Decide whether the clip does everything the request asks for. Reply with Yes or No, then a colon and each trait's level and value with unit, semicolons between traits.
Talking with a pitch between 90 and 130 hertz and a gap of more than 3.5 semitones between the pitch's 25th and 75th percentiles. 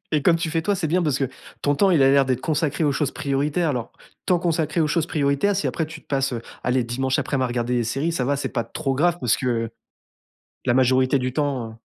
No: medium, 140 Hz; average, 3.9 semitones